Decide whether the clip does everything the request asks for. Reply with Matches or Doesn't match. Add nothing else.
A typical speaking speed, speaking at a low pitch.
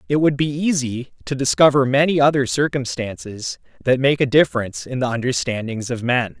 Matches